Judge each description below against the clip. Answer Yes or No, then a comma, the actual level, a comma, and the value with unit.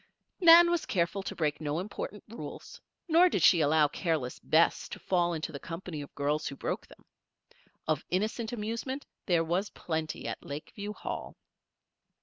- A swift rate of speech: No, average, 160 wpm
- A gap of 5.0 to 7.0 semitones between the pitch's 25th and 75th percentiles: Yes, wide, 5.5 semitones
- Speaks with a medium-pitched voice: Yes, medium, 175 Hz